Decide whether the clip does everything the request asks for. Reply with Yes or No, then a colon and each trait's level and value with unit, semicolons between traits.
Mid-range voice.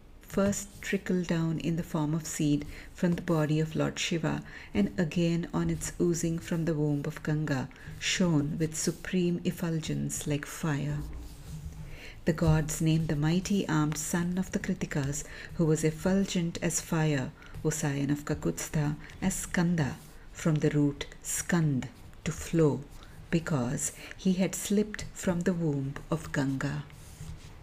Yes: medium, 160 Hz